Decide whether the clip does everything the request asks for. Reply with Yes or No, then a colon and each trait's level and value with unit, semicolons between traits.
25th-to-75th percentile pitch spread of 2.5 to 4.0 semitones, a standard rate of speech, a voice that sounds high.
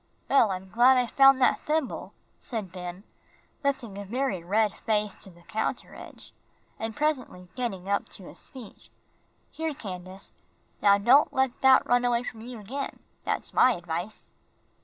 No: average, 5.2 semitones; average, 160 wpm; high, 225 Hz